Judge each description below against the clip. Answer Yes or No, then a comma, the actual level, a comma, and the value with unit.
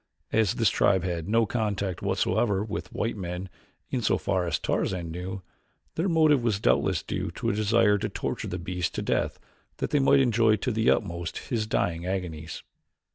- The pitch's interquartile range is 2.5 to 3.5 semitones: No, average, 4.2 semitones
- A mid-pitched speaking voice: No, low, 100 Hz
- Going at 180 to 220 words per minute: Yes, average, 185 wpm